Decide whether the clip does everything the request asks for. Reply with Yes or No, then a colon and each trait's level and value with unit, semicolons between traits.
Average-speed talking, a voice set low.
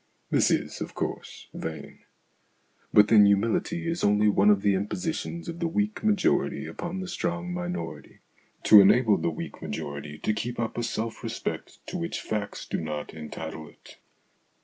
Yes: average, 165 wpm; low, 110 Hz